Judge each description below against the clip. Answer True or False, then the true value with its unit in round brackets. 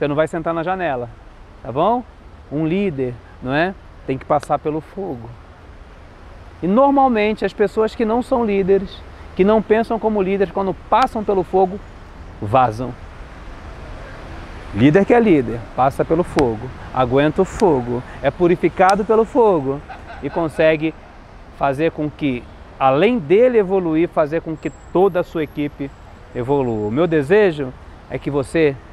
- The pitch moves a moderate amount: False (8.0 semitones)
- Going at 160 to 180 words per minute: False (145 wpm)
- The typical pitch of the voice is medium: True (155 Hz)